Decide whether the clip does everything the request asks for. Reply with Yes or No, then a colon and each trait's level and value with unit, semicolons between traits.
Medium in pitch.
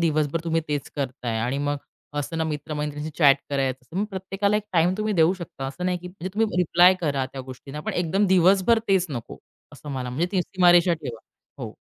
Yes: medium, 160 Hz